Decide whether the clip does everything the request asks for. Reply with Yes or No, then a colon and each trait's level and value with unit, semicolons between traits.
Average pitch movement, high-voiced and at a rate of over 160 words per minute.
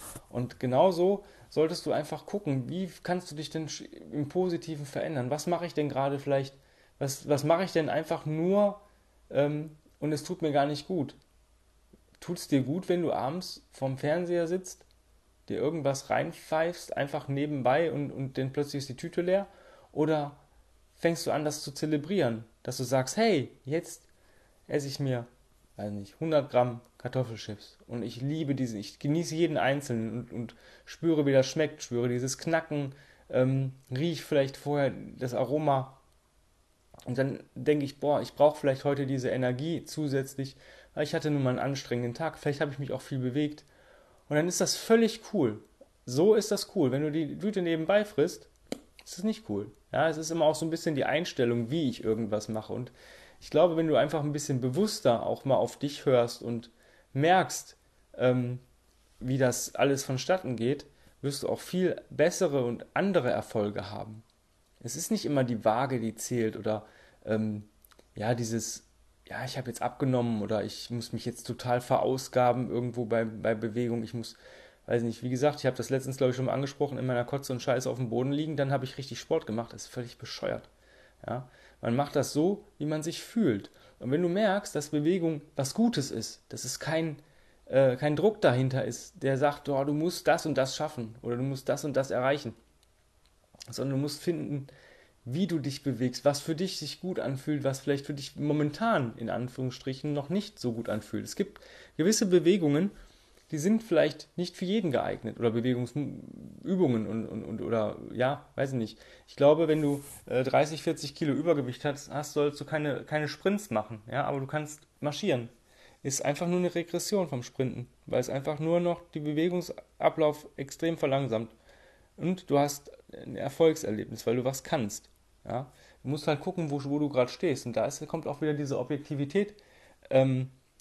No: average, 4.2 semitones; medium, 140 Hz; average, 185 wpm